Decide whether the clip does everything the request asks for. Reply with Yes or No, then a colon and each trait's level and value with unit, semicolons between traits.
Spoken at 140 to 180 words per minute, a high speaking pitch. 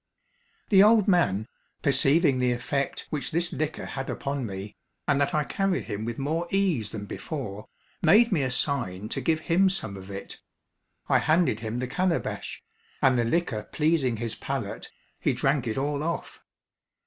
No: average, 170 wpm; medium, 140 Hz